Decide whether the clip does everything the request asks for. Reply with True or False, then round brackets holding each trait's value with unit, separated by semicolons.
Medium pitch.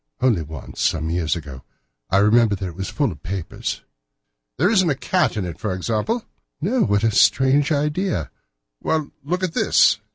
False (115 Hz)